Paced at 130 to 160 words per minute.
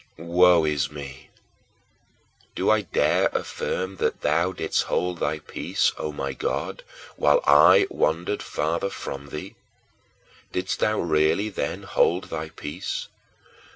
Yes: slow, 135 wpm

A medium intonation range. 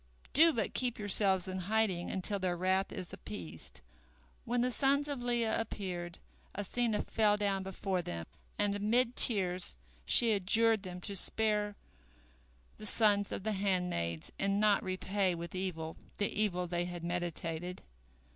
Yes: average, 3.3 semitones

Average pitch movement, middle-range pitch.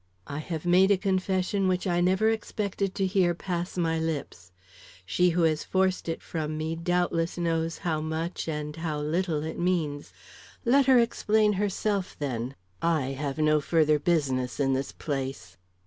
Yes: average, 3.5 semitones; medium, 165 Hz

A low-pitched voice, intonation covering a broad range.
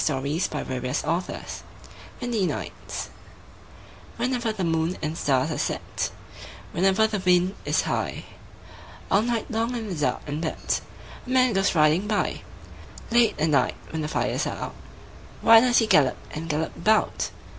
No: medium, 185 Hz; wide, 6.4 semitones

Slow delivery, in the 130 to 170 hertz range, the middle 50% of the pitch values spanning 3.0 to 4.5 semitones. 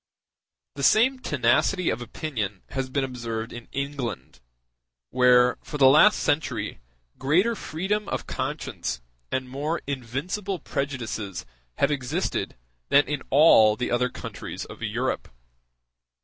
Yes: slow, 120 wpm; low, 135 Hz; average, 4.1 semitones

